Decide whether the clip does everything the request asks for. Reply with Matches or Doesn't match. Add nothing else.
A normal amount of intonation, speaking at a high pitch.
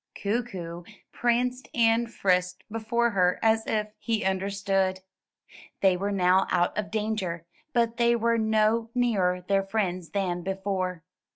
Matches